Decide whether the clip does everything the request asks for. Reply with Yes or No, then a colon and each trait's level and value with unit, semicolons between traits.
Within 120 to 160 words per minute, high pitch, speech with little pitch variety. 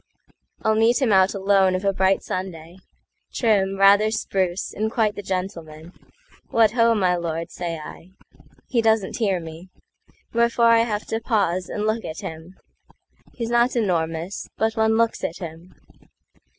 No: average, 140 wpm; high, 195 Hz; average, 3.9 semitones